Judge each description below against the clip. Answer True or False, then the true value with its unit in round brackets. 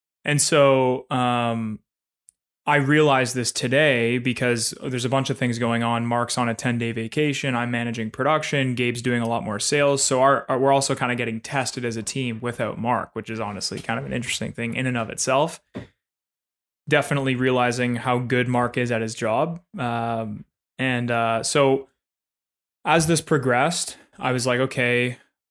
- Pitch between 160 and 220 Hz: False (125 Hz)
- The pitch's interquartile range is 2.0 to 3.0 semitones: True (2.5 semitones)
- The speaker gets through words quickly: False (180 wpm)